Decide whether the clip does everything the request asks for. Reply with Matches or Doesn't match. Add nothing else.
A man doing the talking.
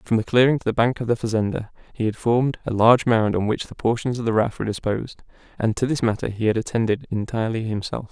Matches